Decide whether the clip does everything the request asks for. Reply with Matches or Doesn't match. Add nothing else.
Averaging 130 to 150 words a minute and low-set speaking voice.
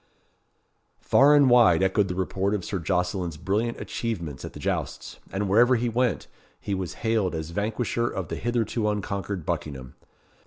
Doesn't match